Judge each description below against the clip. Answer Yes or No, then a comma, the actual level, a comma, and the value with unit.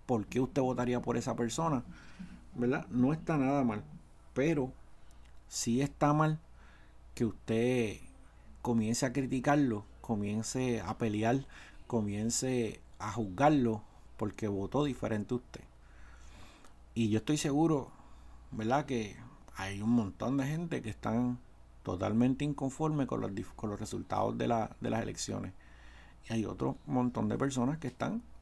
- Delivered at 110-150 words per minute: Yes, average, 135 wpm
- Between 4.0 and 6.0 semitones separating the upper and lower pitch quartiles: Yes, average, 4.7 semitones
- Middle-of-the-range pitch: No, low, 120 Hz